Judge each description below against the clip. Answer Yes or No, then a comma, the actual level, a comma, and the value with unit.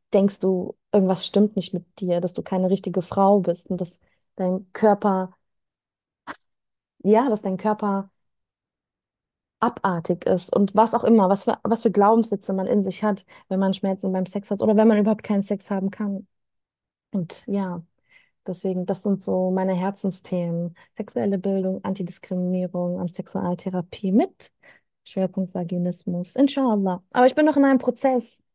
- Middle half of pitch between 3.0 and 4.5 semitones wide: No, narrow, 2.4 semitones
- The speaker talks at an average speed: Yes, average, 155 wpm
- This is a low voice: No, high, 195 Hz